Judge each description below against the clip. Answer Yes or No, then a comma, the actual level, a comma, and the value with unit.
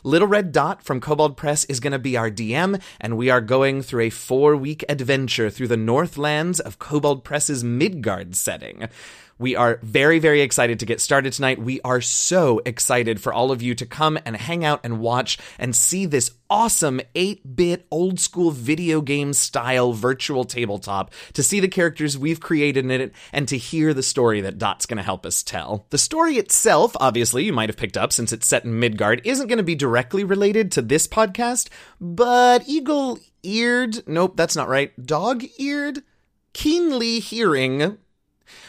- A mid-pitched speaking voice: Yes, medium, 145 Hz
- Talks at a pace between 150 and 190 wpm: Yes, average, 185 wpm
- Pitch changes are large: Yes, wide, 6.5 semitones